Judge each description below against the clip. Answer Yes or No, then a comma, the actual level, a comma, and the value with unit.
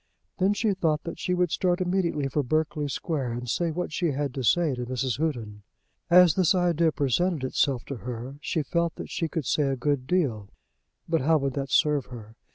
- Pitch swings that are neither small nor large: Yes, average, 4.8 semitones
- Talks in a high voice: No, medium, 150 Hz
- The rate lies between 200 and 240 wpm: Yes, fast, 205 wpm